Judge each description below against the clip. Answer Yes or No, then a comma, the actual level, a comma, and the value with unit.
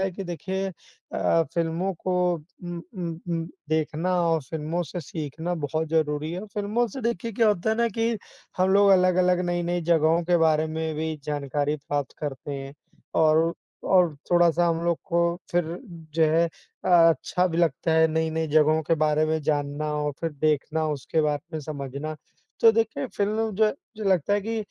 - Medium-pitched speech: Yes, medium, 165 Hz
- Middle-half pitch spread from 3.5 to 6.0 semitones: No, average, 2.9 semitones